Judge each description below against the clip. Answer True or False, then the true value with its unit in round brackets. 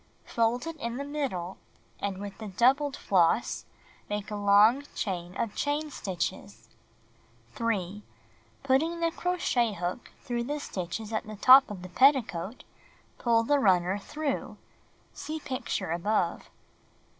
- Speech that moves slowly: False (145 wpm)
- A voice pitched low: False (230 Hz)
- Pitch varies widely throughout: True (6.0 semitones)